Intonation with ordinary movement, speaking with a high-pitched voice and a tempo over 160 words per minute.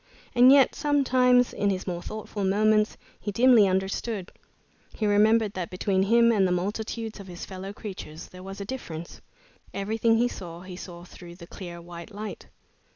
Yes: average, 3.6 semitones; high, 200 Hz; average, 175 wpm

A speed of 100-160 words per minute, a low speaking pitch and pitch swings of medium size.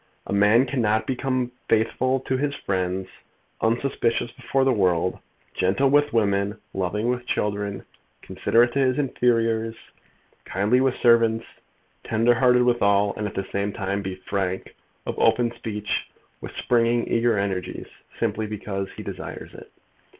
Yes: average, 145 wpm; low, 115 Hz; average, 3.5 semitones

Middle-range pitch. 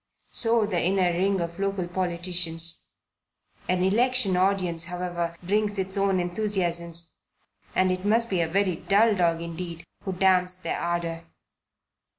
Yes: medium, 180 Hz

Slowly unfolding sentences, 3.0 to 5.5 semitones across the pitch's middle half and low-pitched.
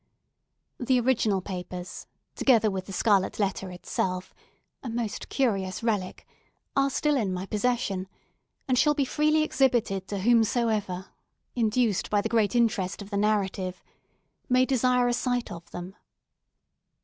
No: slow, 130 wpm; average, 4.5 semitones; high, 215 Hz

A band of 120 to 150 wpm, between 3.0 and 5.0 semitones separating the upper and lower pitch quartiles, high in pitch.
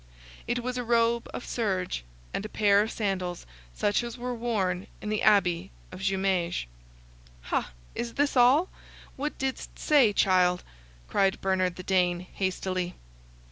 Yes: average, 145 wpm; average, 4.5 semitones; high, 200 Hz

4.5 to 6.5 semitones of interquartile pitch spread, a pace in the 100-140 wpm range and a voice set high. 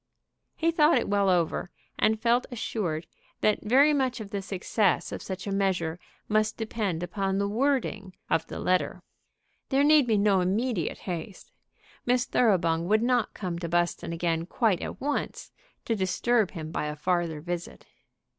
No: average, 5.0 semitones; average, 165 wpm; high, 200 Hz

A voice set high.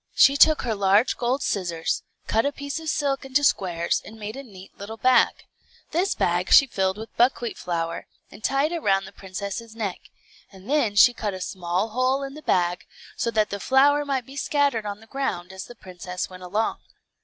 Yes: high, 220 Hz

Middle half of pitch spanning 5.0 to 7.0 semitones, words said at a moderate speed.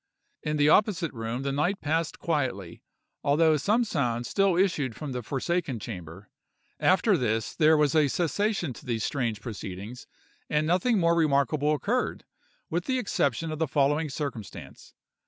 Yes: wide, 5.4 semitones; average, 155 wpm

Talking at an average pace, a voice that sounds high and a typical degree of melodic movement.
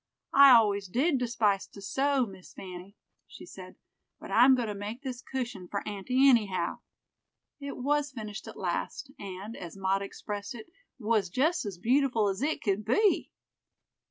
Yes: average, 160 wpm; high, 220 Hz; average, 5.0 semitones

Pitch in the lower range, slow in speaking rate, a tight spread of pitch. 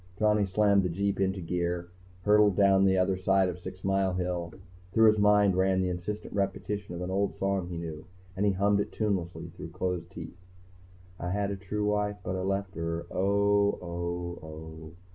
No: very low, 95 Hz; average, 190 wpm; narrow, 2.3 semitones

